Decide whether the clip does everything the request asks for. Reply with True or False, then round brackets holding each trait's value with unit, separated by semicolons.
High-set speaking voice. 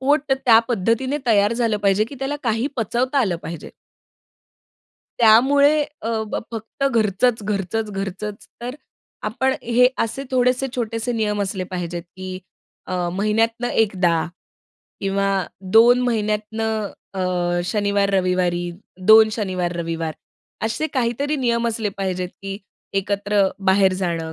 True (215 Hz)